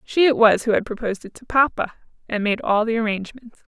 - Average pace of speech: No, fast, 225 wpm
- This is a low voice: No, high, 225 Hz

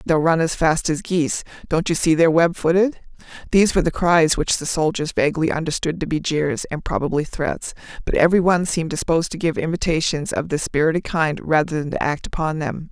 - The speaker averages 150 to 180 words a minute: No, fast, 205 wpm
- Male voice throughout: No, female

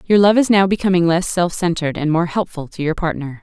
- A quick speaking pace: Yes, fast, 245 wpm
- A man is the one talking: No, female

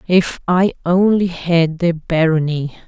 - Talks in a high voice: No, medium, 170 Hz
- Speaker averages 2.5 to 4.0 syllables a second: Yes, 3.7 syllables/s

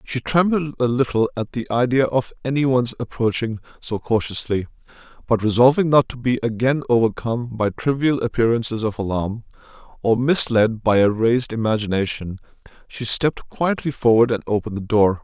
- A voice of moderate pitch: No, low, 120 Hz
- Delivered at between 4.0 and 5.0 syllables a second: No, 5.3 syllables/s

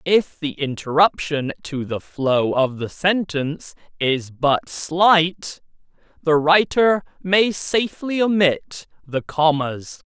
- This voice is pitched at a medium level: Yes, medium, 160 Hz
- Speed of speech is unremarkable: No, slow, 115 wpm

